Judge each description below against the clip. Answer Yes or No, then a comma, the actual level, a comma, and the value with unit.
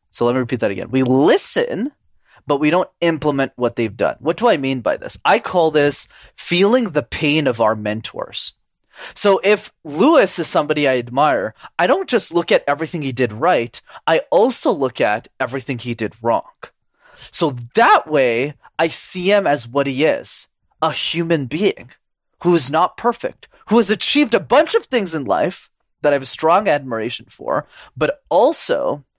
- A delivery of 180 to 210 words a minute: Yes, average, 185 wpm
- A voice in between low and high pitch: Yes, medium, 150 Hz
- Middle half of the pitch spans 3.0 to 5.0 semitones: No, wide, 5.6 semitones